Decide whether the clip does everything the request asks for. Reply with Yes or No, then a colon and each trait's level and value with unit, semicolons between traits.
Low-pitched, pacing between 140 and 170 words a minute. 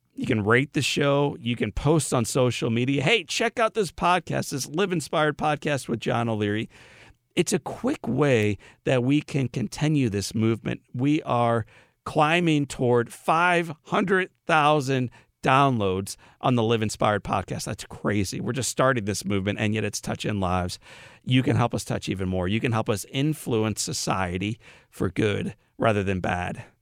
Yes: low, 125 Hz; average, 165 wpm